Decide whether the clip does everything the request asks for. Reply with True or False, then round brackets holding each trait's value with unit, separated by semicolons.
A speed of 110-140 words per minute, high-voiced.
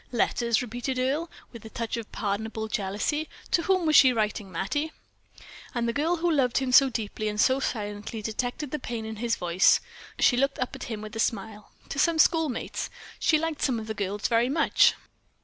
False (200 wpm; 235 Hz)